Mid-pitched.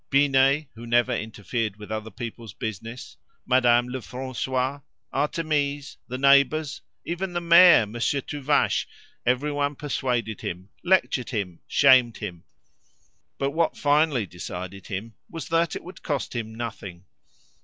No: low, 130 Hz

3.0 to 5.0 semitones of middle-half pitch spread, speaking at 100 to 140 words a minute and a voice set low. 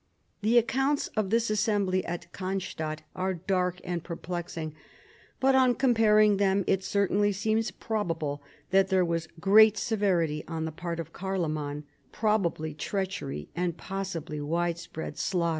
No: average, 3.8 semitones; slow, 135 wpm; medium, 185 Hz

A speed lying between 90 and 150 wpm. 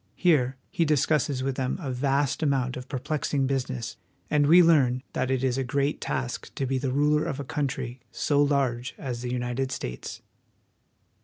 No: average, 175 wpm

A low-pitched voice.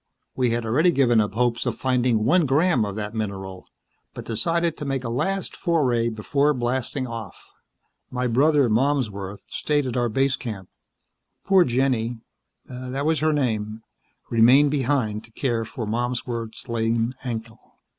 Yes: low, 120 Hz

